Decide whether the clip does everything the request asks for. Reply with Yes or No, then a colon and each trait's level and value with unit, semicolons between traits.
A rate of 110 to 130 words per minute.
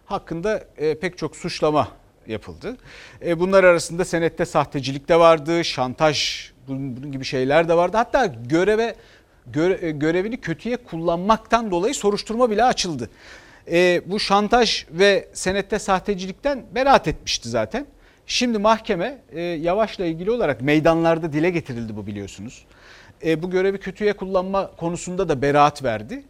Yes: average, 120 wpm